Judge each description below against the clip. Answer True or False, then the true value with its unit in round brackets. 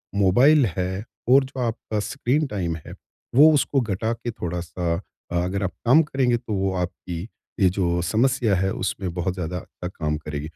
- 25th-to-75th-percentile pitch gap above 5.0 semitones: True (5.4 semitones)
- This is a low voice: True (95 Hz)